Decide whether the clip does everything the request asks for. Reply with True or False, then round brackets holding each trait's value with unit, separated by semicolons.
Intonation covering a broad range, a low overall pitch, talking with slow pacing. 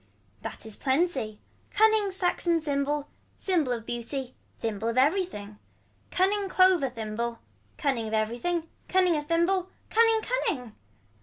False (7.9 semitones; 295 Hz; 125 wpm)